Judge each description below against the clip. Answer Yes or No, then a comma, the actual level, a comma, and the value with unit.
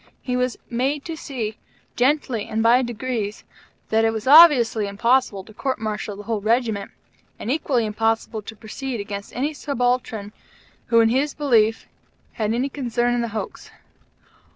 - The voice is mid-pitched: No, high, 235 Hz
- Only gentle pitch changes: No, average, 3.1 semitones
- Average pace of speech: Yes, average, 155 wpm